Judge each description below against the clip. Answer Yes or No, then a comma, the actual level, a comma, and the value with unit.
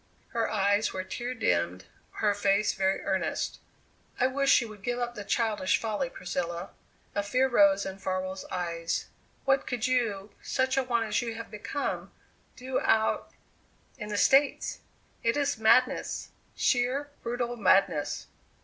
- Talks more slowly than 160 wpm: Yes, average, 150 wpm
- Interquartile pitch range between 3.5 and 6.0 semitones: Yes, average, 4.3 semitones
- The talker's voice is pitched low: No, high, 220 Hz